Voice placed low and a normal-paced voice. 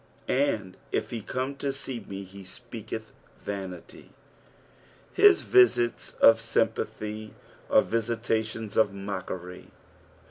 No: low, 110 Hz; slow, 105 wpm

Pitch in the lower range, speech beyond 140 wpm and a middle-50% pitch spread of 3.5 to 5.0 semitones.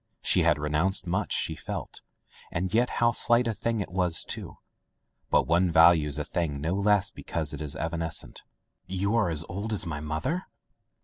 Yes: very low, 90 Hz; average, 180 wpm; average, 4.5 semitones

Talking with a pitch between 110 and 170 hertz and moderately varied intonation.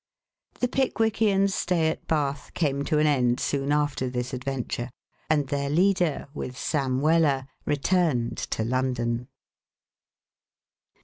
Yes: medium, 140 Hz; average, 4.1 semitones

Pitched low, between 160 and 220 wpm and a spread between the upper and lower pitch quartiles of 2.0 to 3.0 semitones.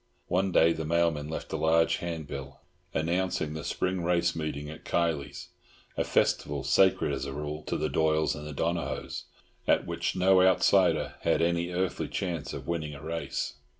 Yes: very low, 80 Hz; average, 170 wpm; narrow, 2.5 semitones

